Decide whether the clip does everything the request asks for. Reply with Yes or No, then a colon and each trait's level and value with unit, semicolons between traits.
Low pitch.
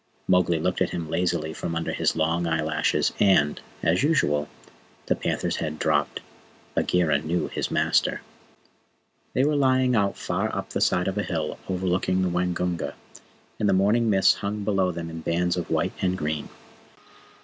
Yes: very low, 90 Hz